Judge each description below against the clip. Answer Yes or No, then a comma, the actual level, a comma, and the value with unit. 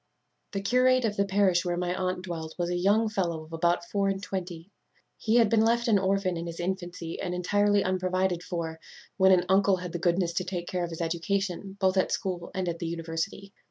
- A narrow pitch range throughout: Yes, narrow, 2.3 semitones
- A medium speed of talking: No, fast, 225 wpm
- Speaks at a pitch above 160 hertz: Yes, medium, 185 Hz